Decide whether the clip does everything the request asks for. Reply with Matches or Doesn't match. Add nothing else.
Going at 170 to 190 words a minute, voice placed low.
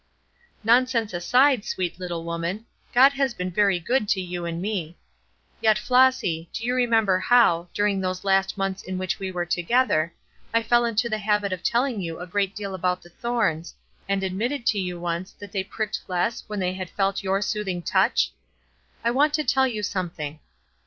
Doesn't match